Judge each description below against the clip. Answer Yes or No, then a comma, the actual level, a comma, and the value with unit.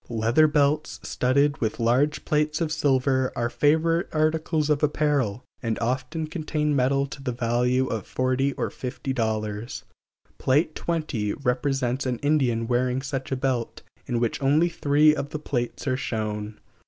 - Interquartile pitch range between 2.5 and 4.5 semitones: Yes, average, 3.8 semitones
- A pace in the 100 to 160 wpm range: Yes, average, 155 wpm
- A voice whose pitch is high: No, low, 135 Hz